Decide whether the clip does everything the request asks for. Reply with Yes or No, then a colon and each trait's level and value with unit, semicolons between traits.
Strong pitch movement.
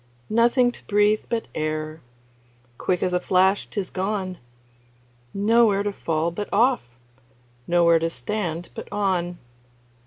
No: average, 3.6 semitones